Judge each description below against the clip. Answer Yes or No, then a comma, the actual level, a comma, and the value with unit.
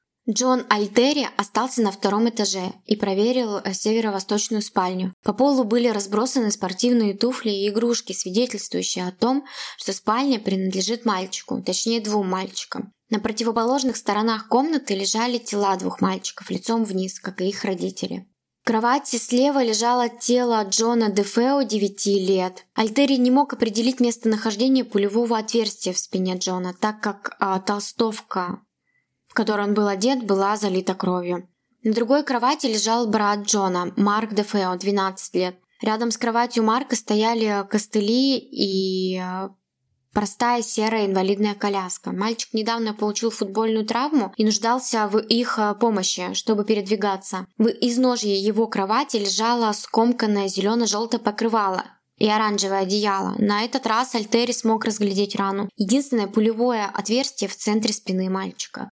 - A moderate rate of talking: Yes, average, 135 wpm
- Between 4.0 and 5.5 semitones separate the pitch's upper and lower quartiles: No, average, 2.9 semitones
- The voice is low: No, high, 215 Hz